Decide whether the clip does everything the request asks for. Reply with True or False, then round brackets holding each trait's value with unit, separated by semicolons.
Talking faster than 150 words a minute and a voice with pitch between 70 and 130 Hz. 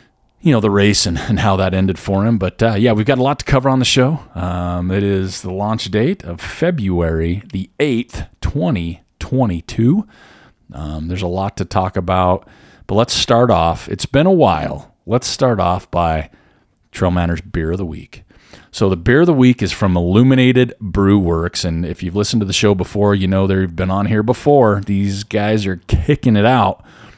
True (200 wpm; 100 Hz)